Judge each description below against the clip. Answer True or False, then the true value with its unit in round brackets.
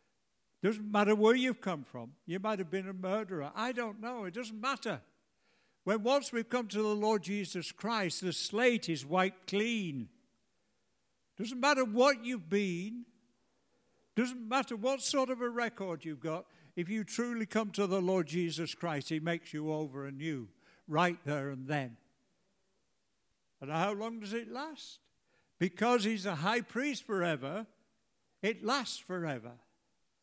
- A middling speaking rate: True (155 wpm)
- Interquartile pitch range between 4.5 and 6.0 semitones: True (5.5 semitones)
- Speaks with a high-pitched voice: True (205 Hz)